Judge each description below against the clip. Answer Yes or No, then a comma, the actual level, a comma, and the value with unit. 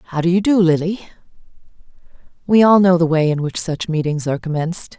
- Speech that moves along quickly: No, average, 195 wpm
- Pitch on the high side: No, medium, 170 Hz